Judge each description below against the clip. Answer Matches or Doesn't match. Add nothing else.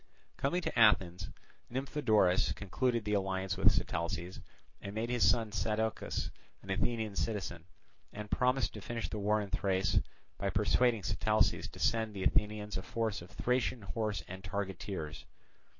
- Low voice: Matches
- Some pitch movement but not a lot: Matches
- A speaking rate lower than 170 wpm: Matches